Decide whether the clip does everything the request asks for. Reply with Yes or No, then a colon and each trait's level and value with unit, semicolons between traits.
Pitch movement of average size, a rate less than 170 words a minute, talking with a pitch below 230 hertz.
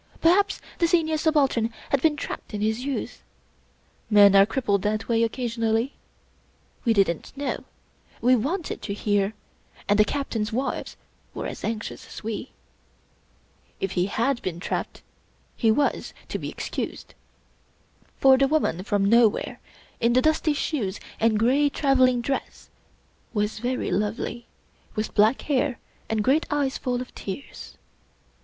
No: average, 4.7 semitones; average, 140 wpm; high, 235 Hz